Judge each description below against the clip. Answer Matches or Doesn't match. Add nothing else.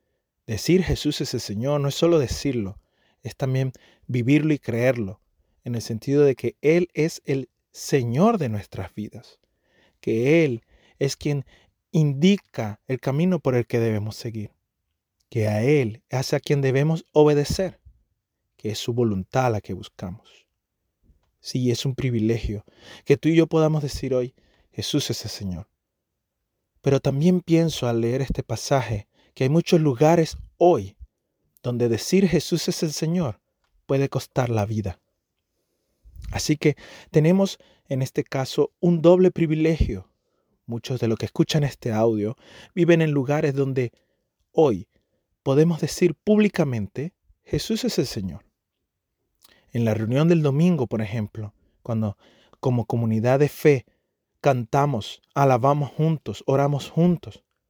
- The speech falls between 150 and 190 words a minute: Doesn't match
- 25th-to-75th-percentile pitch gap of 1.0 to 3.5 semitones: Doesn't match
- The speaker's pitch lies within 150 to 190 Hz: Doesn't match